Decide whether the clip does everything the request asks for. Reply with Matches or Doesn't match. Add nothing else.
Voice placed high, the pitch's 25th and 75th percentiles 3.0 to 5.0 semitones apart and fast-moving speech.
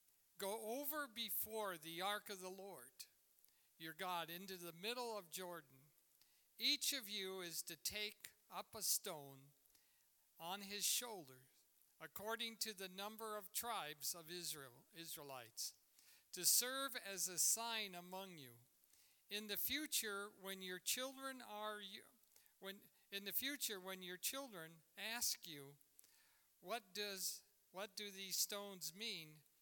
Doesn't match